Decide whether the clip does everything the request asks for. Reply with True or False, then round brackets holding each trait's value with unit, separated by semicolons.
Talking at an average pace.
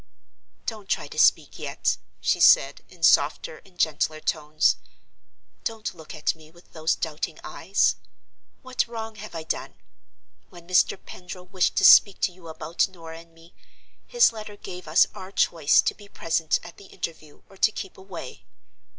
True (165 wpm)